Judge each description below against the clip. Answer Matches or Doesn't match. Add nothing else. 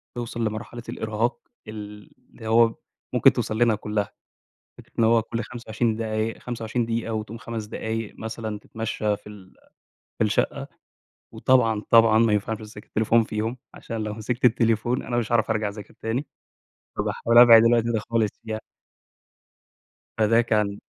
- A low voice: Matches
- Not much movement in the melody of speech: Matches